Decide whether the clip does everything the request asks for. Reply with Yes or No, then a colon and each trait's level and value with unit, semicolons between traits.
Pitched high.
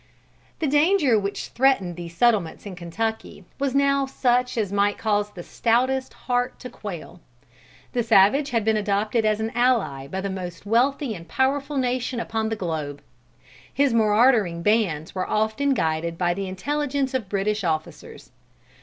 Yes: high, 220 Hz